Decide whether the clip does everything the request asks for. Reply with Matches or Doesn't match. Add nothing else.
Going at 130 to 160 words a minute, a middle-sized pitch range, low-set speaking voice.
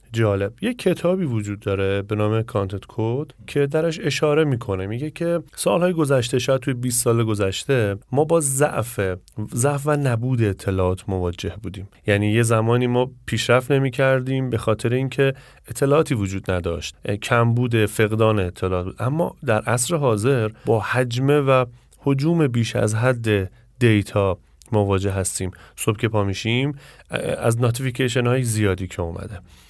Matches